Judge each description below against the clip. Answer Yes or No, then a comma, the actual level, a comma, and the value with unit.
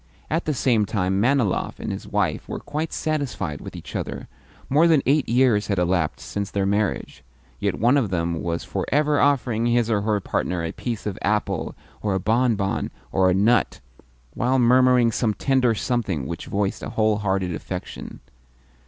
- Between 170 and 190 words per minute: Yes, average, 180 wpm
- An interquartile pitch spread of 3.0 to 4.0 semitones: No, average, 4.8 semitones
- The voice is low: Yes, low, 110 Hz